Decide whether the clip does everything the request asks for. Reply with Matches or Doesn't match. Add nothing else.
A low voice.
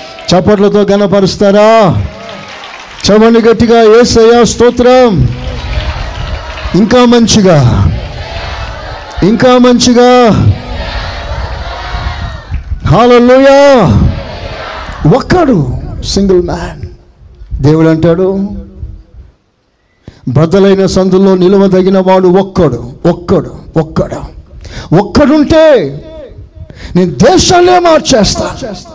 Doesn't match